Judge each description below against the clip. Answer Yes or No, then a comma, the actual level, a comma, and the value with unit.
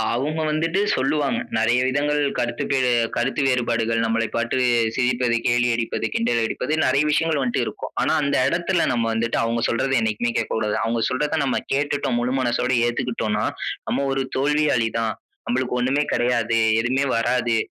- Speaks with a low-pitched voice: Yes, low, 125 Hz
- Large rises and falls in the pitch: No, average, 3.2 semitones